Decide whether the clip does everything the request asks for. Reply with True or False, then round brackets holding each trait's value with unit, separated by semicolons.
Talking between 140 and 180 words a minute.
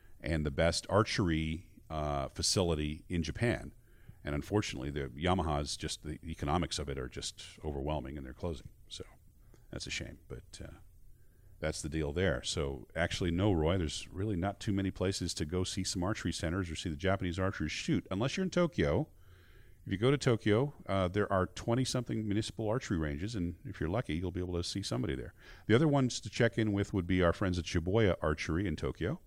False (200 wpm)